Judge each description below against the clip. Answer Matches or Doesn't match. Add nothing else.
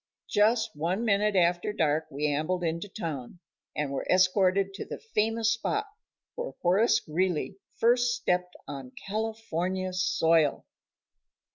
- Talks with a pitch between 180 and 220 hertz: Matches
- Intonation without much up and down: Doesn't match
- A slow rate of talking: Matches